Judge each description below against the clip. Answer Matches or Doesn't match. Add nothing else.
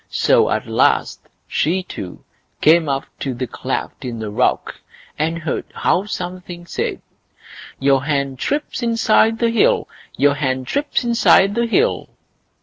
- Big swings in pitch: Matches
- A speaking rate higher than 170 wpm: Doesn't match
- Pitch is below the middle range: Doesn't match